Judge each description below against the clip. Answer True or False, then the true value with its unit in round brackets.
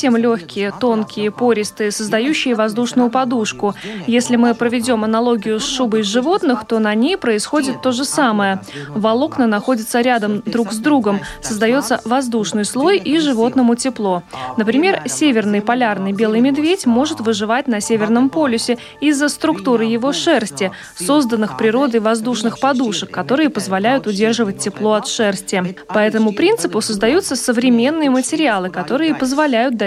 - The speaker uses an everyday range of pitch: True (3.5 semitones)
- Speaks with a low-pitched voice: False (235 Hz)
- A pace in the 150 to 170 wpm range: False (130 wpm)